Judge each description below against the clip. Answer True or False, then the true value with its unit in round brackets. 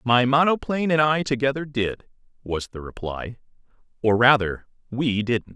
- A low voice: True (125 Hz)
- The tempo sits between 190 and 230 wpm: False (140 wpm)